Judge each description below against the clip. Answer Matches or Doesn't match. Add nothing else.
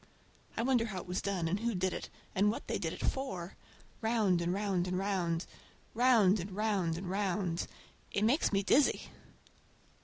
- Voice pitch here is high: Matches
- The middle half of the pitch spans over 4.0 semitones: Doesn't match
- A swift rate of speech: Doesn't match